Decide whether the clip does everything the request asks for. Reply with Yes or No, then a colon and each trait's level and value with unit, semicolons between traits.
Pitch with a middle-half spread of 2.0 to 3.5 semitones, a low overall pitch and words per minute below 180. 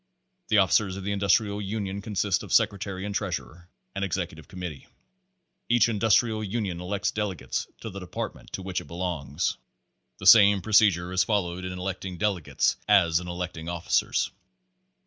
Yes: narrow, 2.6 semitones; very low, 95 Hz; average, 155 wpm